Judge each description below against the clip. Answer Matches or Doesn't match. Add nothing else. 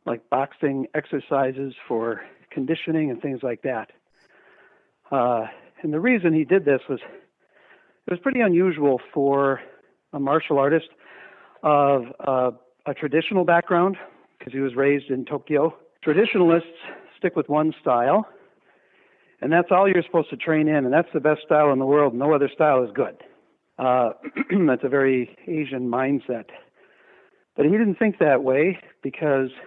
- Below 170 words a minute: Matches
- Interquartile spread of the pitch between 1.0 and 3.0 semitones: Doesn't match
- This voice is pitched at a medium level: Matches